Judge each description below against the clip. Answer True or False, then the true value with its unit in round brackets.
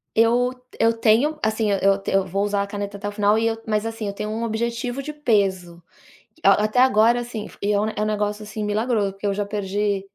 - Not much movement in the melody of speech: True (2.0 semitones)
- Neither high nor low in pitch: False (210 Hz)